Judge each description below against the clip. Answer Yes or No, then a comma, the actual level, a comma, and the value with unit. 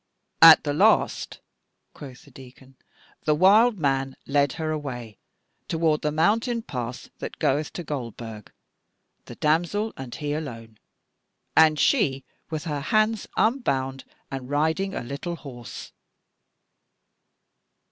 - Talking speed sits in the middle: No, slow, 120 wpm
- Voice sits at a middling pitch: Yes, medium, 150 Hz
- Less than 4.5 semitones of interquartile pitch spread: Yes, average, 3.9 semitones